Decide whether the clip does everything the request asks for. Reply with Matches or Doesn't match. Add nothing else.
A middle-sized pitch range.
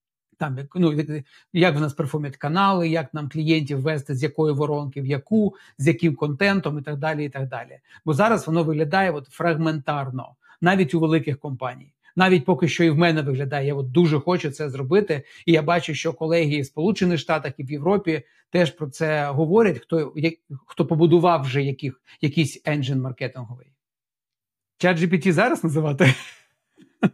Matches